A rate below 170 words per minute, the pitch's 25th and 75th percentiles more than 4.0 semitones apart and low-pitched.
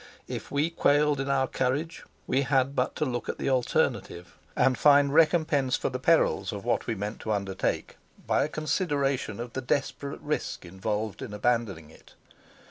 No: average, 175 wpm; average, 4.4 semitones; low, 130 Hz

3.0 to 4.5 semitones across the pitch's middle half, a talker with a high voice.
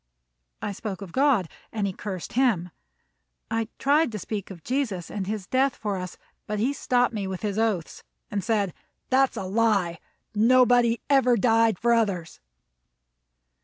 Yes: average, 4.2 semitones; high, 215 Hz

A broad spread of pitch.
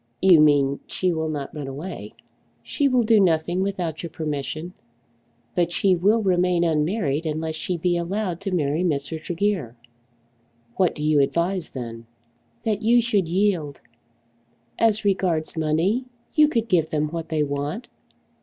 No: average, 4.2 semitones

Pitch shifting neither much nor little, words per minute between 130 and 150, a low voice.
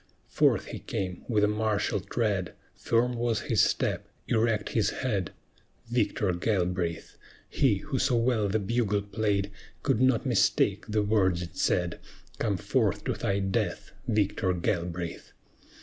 Yes: average, 3.4 semitones; average, 140 wpm; low, 105 Hz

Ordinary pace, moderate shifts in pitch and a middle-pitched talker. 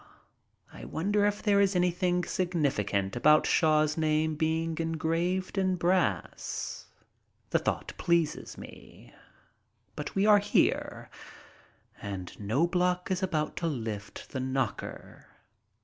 No: slow, 115 wpm; average, 3.7 semitones; medium, 165 Hz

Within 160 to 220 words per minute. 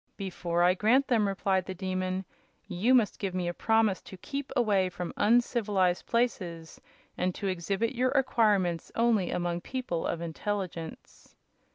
No: average, 150 wpm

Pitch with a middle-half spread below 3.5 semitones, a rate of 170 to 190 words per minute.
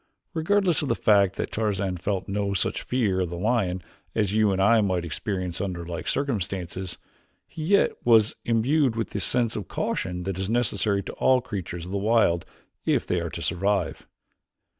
No: average, 3.9 semitones; average, 185 wpm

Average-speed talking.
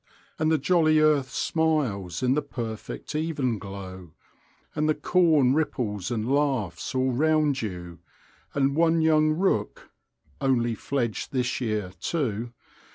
No: slow, 125 wpm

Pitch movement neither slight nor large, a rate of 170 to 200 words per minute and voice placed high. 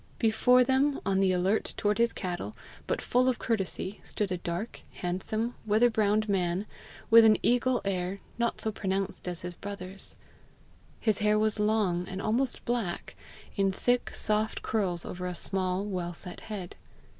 No: average, 3.3 semitones; average, 160 wpm; high, 205 Hz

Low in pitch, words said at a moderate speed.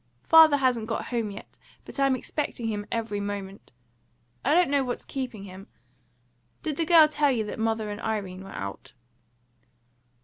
No: high, 230 Hz; average, 165 wpm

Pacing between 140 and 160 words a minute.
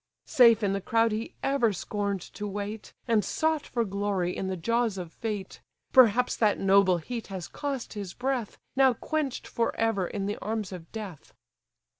No: average, 175 wpm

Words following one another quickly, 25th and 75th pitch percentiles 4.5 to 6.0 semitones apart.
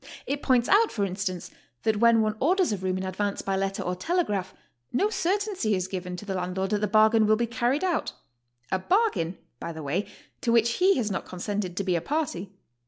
Yes: fast, 225 wpm; average, 5.1 semitones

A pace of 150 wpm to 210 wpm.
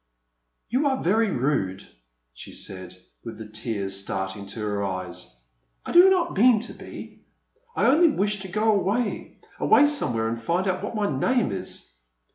Yes: average, 170 wpm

